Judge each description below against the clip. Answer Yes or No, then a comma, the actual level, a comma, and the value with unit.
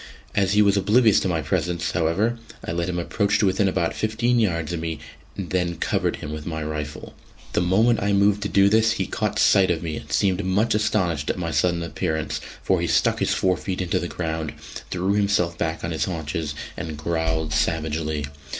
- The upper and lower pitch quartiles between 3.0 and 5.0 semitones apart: Yes, average, 3.7 semitones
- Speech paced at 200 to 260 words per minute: Yes, fast, 205 wpm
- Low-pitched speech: Yes, very low, 85 Hz